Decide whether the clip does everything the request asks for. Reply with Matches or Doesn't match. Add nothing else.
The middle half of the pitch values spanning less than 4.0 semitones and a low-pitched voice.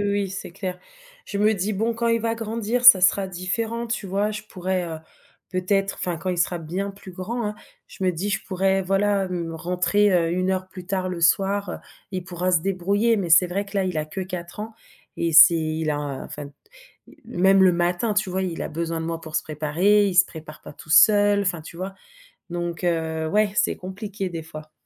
Doesn't match